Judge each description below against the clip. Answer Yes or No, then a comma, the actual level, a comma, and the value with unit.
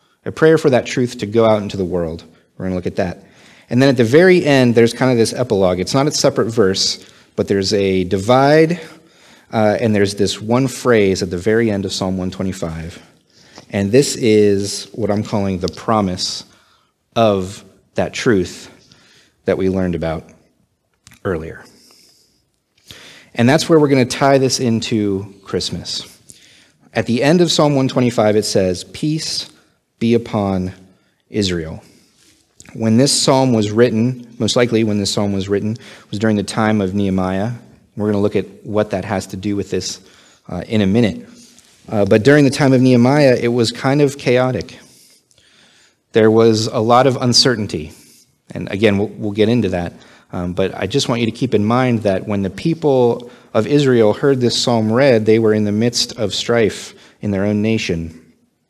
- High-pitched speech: No, low, 110 Hz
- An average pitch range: Yes, average, 4.0 semitones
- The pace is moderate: Yes, average, 180 wpm